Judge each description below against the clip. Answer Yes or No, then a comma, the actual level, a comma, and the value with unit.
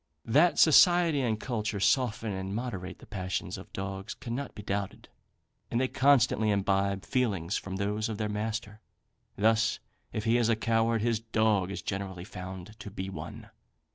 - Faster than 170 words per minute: No, average, 165 wpm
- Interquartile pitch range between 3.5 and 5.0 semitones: No, average, 3.0 semitones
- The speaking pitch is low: Yes, low, 110 Hz